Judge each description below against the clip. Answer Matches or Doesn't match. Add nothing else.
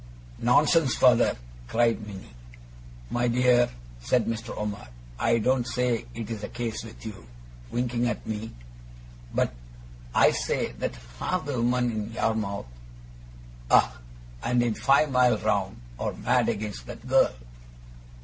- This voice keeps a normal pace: Doesn't match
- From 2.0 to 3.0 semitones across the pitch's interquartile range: Matches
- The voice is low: Matches